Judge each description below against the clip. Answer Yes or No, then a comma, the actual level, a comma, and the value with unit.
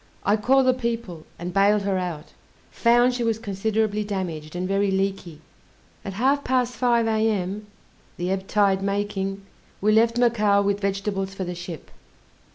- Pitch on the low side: No, high, 200 Hz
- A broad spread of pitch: No, average, 2.8 semitones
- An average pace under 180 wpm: Yes, average, 160 wpm